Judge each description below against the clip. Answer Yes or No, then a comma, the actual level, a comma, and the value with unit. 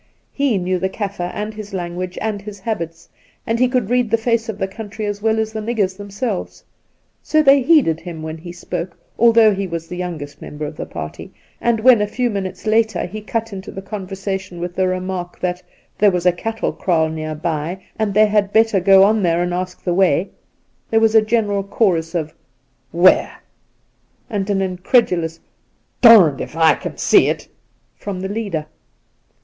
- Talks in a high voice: Yes, high, 195 Hz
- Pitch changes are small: No, average, 3.8 semitones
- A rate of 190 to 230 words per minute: Yes, average, 200 wpm